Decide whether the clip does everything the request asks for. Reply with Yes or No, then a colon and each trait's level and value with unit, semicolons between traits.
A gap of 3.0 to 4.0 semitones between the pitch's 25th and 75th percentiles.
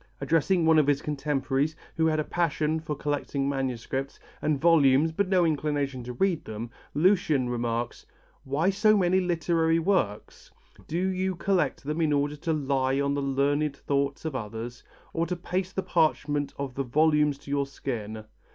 Yes: average, 3.3 semitones